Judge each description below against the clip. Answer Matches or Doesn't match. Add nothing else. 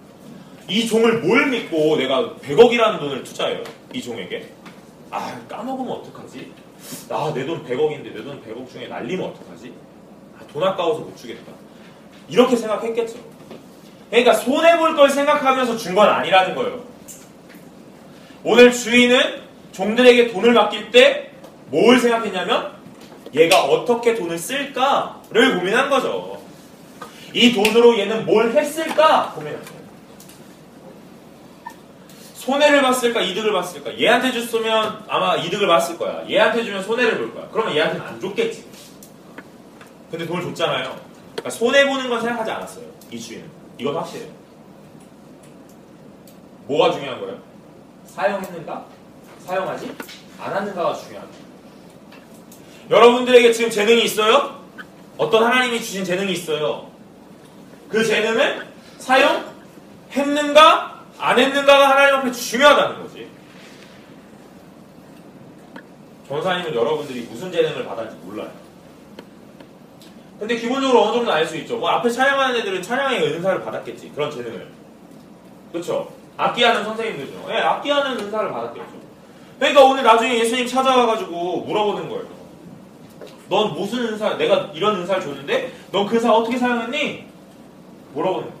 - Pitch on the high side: Matches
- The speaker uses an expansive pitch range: Doesn't match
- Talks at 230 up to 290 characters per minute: Doesn't match